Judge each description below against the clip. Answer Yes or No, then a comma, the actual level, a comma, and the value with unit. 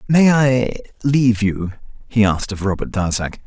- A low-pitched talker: Yes, low, 110 Hz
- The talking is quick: No, average, 155 wpm